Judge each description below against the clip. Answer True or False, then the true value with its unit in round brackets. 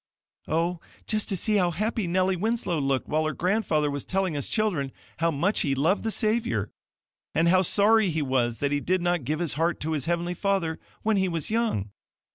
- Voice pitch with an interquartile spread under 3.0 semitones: False (4.8 semitones)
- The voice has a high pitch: False (175 Hz)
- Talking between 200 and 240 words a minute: True (205 wpm)